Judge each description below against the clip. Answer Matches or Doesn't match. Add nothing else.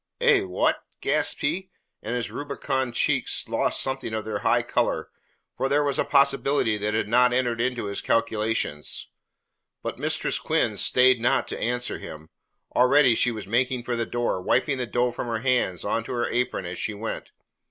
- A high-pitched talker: Doesn't match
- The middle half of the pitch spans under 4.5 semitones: Matches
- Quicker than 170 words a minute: Matches